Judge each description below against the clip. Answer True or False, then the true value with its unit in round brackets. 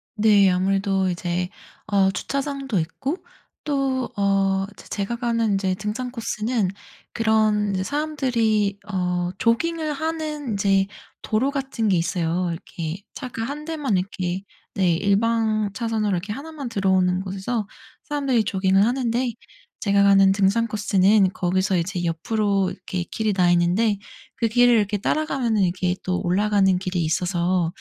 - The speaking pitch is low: False (205 Hz)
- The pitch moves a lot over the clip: False (3.9 semitones)